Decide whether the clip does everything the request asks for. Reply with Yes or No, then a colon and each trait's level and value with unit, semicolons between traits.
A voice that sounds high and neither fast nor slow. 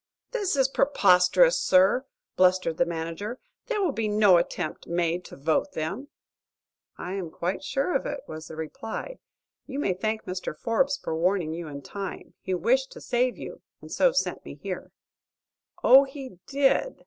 Yes: high, 200 Hz; average, 170 wpm